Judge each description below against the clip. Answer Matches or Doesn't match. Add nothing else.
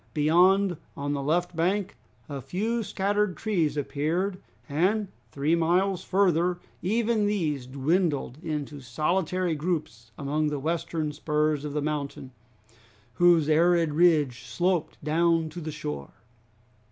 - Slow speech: Matches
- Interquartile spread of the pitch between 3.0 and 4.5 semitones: Matches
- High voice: Doesn't match